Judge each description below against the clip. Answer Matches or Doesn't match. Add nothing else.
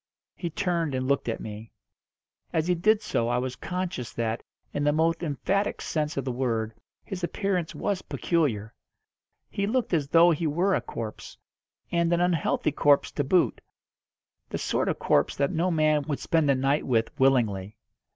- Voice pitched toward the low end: Doesn't match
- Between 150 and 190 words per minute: Matches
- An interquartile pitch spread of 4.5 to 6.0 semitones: Matches